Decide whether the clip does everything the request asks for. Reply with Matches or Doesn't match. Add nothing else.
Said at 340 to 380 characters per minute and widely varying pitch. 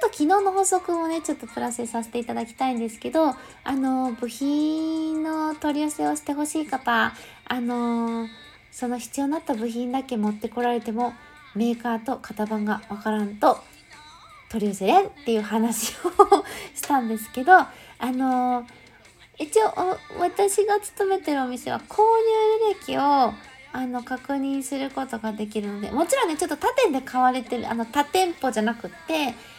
Doesn't match